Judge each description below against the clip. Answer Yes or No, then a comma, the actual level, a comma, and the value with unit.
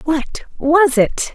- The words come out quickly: No, slow, 135 wpm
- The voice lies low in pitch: No, very high, 305 Hz